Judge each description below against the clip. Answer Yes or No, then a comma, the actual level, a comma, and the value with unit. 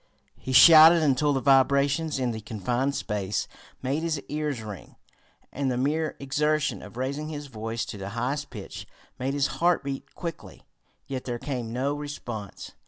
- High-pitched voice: No, low, 135 Hz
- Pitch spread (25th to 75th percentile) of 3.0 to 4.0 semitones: Yes, average, 3.5 semitones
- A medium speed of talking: Yes, average, 165 wpm